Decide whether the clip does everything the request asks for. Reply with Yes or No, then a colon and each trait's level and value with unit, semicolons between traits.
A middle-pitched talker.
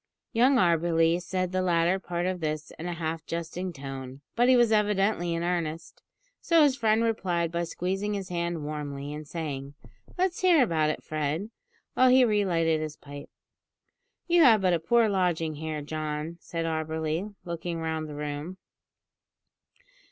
Yes: medium, 170 Hz